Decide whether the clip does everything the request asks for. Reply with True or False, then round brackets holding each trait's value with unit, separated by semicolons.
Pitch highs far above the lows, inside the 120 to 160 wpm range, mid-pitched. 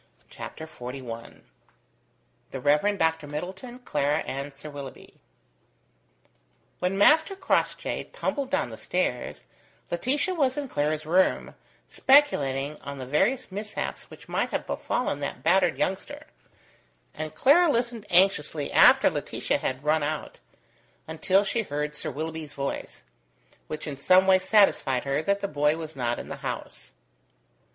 True (6.0 semitones; 135 wpm; 160 Hz)